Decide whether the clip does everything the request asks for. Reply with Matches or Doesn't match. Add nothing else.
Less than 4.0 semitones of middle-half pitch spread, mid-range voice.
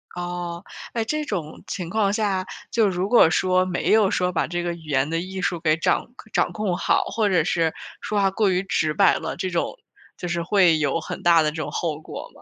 Matches